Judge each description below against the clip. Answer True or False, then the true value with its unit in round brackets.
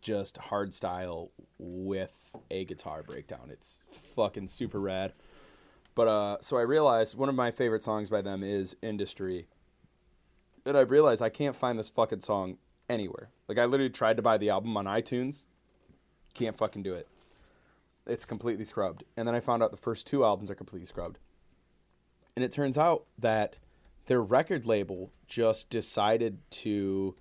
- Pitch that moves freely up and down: False (3.1 semitones)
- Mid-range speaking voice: False (105 Hz)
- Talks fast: False (165 wpm)